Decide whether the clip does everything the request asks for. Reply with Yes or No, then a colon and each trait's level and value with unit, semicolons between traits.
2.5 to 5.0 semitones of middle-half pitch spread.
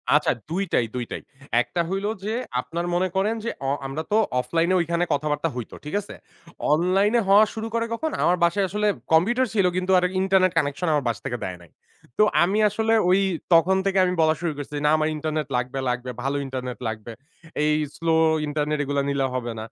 No: wide, 5.4 semitones